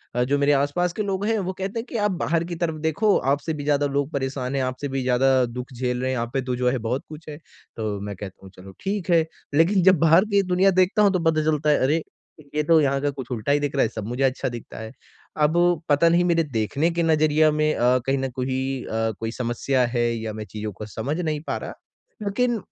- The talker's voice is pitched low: No, medium, 145 Hz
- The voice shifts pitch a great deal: No, average, 5.0 semitones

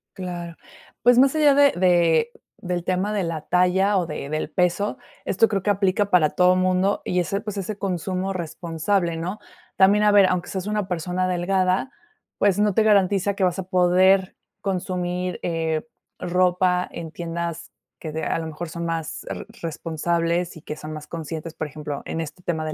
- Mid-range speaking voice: Yes, medium, 180 Hz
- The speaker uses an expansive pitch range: No, narrow, 2.6 semitones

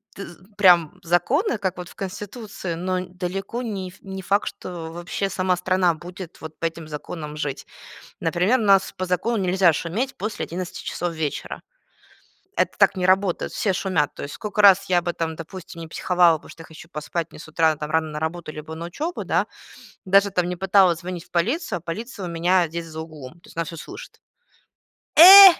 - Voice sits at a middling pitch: Yes, medium, 180 Hz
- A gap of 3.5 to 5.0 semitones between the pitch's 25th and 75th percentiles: No, average, 2.9 semitones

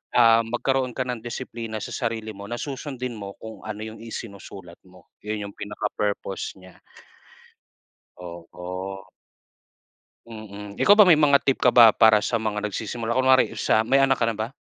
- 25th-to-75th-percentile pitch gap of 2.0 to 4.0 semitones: Yes, average, 3.2 semitones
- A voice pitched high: No, low, 110 Hz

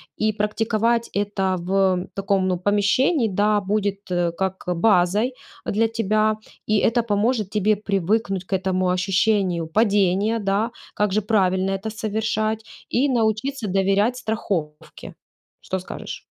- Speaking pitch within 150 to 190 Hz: No, high, 205 Hz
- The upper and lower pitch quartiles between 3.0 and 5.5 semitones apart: No, narrow, 2.5 semitones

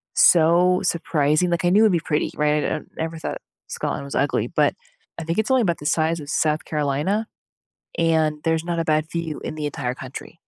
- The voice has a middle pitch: Yes, medium, 160 Hz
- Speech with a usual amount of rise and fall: No, narrow, 2.2 semitones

